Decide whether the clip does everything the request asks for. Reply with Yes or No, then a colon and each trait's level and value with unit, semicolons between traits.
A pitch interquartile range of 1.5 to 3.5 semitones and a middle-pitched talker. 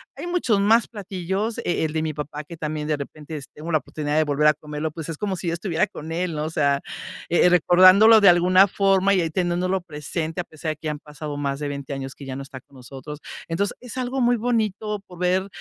No: average, 4.3 semitones; medium, 165 Hz